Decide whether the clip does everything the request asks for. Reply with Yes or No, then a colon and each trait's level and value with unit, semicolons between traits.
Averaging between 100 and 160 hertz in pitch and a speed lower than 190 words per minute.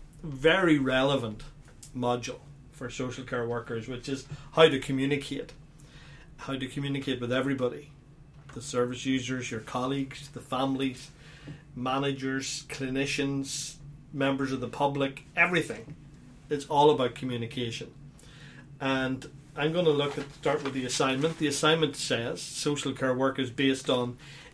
Yes: medium, 140 Hz; slow, 135 wpm